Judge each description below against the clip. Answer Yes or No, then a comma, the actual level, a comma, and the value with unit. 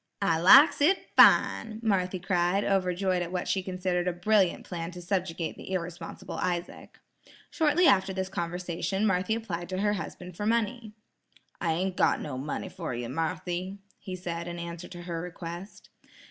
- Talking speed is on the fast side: No, average, 165 wpm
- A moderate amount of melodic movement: No, narrow, 2.1 semitones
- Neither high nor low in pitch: Yes, medium, 180 Hz